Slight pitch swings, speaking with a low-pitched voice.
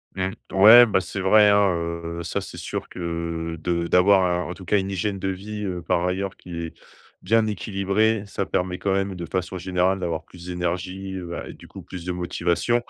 Yes: narrow, 2.2 semitones; very low, 90 Hz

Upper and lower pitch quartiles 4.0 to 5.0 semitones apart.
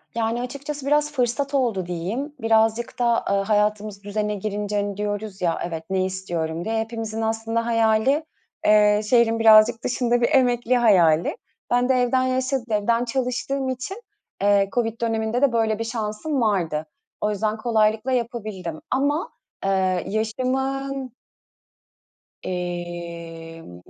No: average, 3.5 semitones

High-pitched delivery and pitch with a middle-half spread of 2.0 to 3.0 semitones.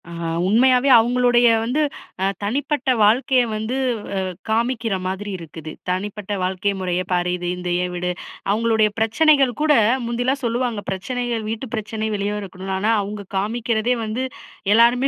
No: high, 220 Hz; average, 3.8 semitones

